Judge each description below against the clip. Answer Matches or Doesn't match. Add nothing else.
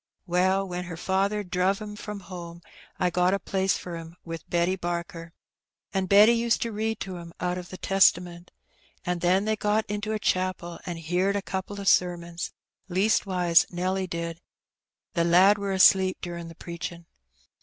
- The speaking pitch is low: Doesn't match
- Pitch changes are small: Matches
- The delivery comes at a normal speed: Matches